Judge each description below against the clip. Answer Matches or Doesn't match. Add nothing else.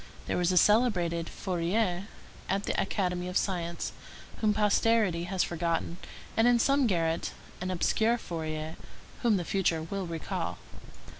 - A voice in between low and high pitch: Matches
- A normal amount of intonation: Matches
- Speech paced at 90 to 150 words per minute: Matches